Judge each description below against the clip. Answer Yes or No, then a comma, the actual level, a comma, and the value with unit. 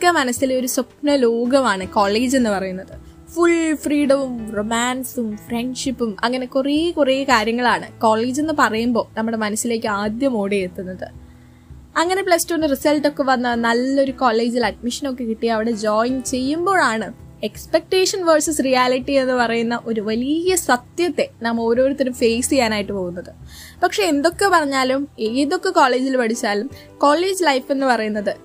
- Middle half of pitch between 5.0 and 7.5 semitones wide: No, average, 4.2 semitones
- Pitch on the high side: Yes, very high, 255 Hz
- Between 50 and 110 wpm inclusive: No, fast, 125 wpm